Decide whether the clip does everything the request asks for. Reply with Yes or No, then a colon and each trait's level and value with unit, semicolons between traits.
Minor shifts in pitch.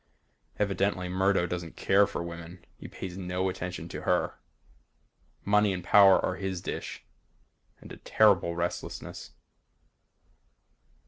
Yes: narrow, 2.0 semitones